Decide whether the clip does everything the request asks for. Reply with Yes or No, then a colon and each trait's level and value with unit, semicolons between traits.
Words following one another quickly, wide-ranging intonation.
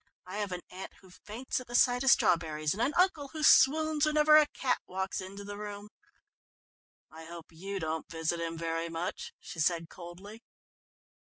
No: average, 180 wpm; wide, 6.9 semitones